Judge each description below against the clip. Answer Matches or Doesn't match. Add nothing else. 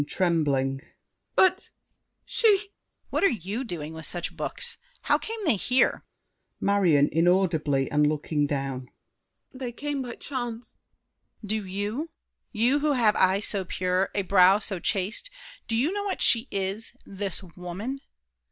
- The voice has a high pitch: Matches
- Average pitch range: Doesn't match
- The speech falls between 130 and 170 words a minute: Matches